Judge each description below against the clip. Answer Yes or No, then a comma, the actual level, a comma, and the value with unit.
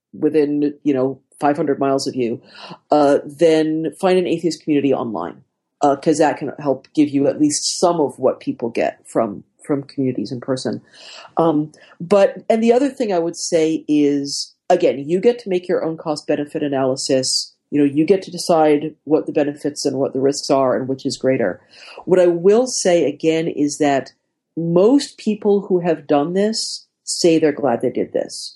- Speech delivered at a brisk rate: No, average, 190 wpm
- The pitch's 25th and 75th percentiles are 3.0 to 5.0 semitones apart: Yes, average, 4.0 semitones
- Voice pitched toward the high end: No, medium, 155 Hz